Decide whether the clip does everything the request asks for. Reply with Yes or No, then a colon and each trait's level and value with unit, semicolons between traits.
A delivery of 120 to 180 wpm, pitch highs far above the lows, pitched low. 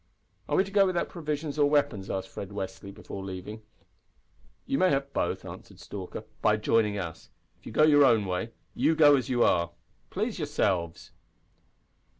Yes: average, 170 wpm; wide, 7.2 semitones; low, 115 Hz